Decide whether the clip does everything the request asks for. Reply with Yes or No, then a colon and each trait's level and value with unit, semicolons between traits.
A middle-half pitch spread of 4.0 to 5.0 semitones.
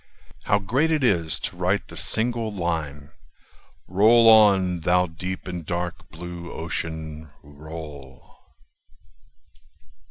Yes: average, 4.3 semitones